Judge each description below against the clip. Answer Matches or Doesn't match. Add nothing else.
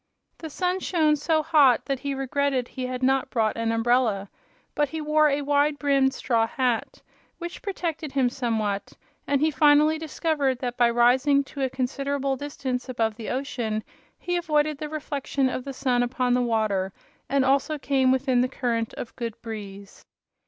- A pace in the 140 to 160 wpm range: Doesn't match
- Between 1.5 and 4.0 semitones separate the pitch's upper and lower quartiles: Matches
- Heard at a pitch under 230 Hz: Doesn't match